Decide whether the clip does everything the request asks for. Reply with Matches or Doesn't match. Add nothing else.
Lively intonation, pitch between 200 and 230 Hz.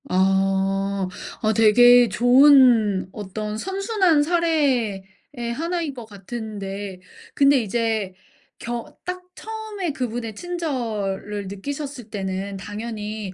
Matches